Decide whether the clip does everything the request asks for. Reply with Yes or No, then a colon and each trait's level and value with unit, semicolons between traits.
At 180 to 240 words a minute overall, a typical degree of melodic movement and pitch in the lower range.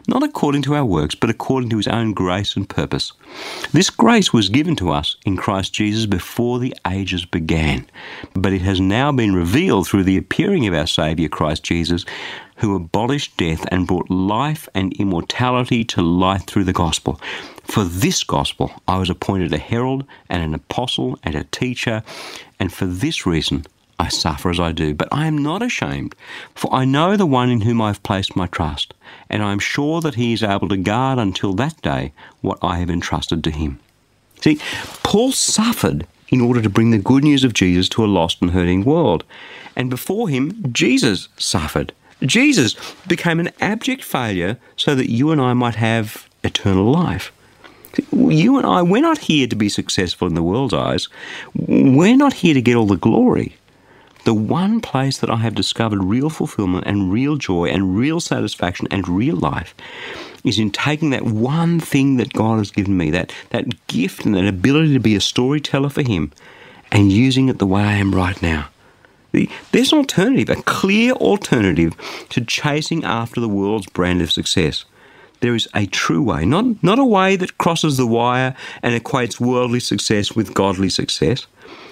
No: average, 190 wpm; wide, 6.5 semitones; low, 110 Hz